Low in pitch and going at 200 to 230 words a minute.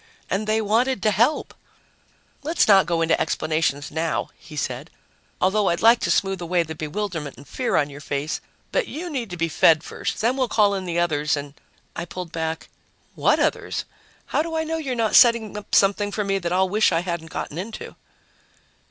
No: high, 190 Hz; fast, 205 wpm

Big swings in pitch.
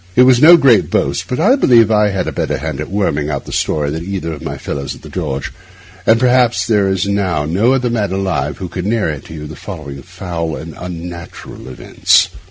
Yes: wide, 6.5 semitones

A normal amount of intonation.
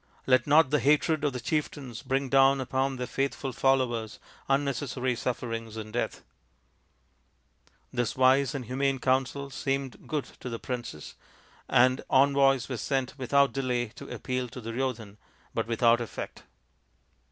No: narrow, 2.2 semitones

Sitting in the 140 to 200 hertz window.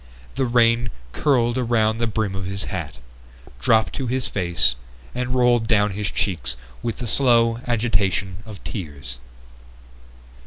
No: low, 110 Hz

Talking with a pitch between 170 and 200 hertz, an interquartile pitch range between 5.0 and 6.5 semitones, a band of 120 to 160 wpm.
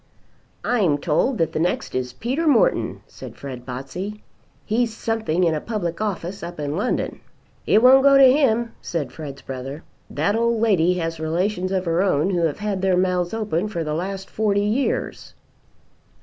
No: medium, 185 Hz; wide, 5.4 semitones; average, 175 wpm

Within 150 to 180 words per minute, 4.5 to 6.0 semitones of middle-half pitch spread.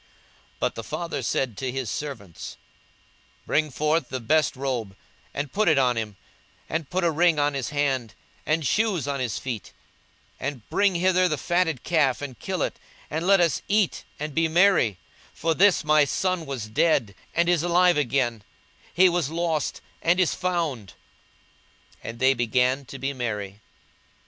Yes: average, 175 wpm; average, 5.2 semitones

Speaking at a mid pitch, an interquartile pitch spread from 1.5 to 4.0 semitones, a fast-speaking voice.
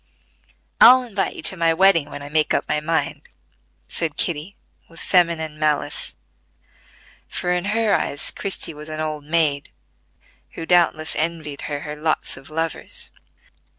No: medium, 160 Hz; narrow, 2.5 semitones; average, 150 wpm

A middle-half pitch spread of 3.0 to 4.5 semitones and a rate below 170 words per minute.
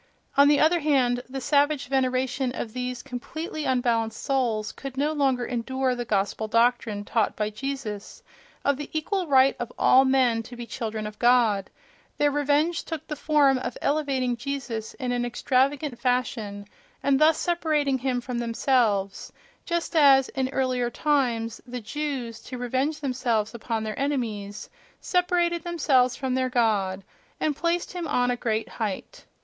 Yes: average, 3.4 semitones; average, 155 wpm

